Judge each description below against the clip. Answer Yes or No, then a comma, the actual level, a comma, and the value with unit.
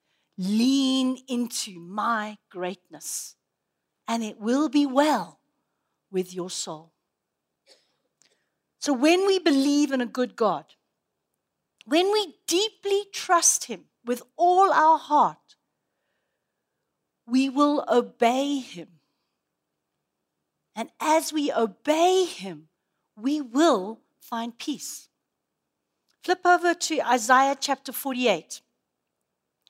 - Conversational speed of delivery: No, slow, 95 wpm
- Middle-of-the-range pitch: No, very high, 265 Hz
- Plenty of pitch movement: Yes, wide, 6.1 semitones